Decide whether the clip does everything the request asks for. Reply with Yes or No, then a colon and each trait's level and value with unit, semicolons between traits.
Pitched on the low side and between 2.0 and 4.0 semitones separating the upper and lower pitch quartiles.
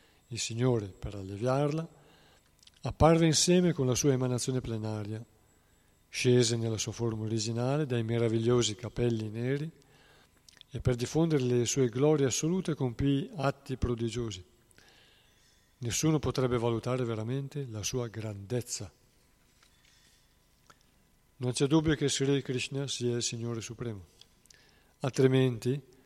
Yes: low, 125 Hz; average, 3.0 semitones